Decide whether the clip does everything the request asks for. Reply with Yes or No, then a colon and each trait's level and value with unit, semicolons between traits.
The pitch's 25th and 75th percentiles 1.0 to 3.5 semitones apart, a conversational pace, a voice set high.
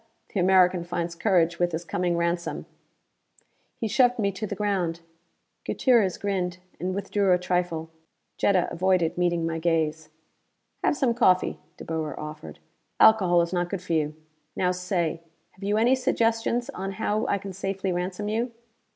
No: average, 3.0 semitones; average, 160 wpm; medium, 180 Hz